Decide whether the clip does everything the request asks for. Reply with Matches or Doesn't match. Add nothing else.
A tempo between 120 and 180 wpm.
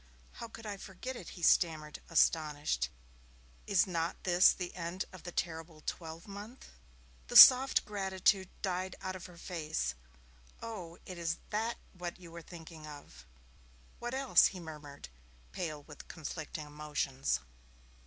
Matches